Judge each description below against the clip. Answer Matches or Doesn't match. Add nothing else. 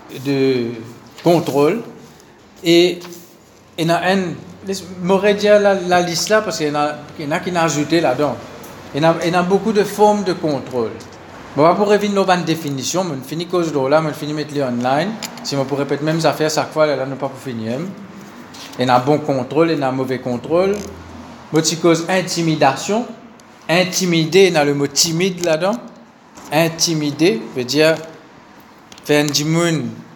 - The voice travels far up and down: Doesn't match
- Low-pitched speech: Doesn't match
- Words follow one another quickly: Matches